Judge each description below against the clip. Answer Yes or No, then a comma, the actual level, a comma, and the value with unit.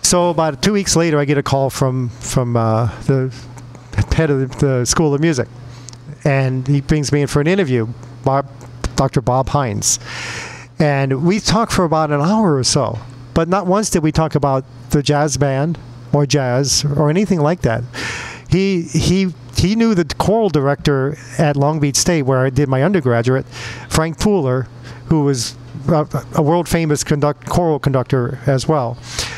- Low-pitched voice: No, medium, 145 Hz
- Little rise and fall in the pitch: No, average, 4.0 semitones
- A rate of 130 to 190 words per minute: Yes, average, 175 wpm